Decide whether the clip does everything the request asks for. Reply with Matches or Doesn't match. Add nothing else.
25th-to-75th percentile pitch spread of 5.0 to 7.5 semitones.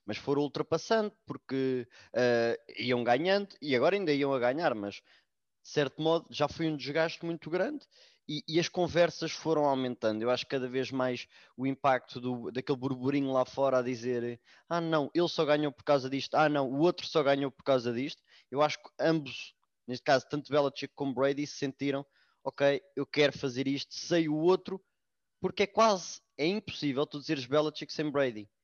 Doesn't match